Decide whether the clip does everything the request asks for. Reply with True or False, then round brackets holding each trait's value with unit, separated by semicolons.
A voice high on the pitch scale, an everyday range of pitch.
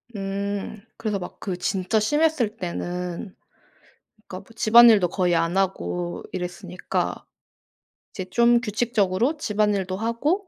True (200 Hz; 4.1 semitones)